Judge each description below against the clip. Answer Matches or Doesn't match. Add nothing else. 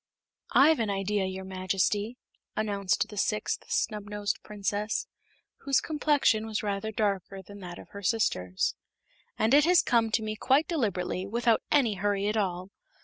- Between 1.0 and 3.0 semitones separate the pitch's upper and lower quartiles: Matches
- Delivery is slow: Doesn't match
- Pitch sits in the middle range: Doesn't match